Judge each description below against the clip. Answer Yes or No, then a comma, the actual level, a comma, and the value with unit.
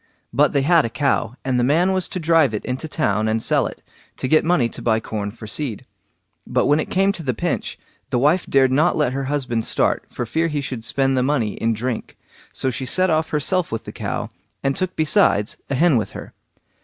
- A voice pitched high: No, low, 135 Hz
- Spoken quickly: Yes, fast, 230 wpm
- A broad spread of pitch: No, average, 5.0 semitones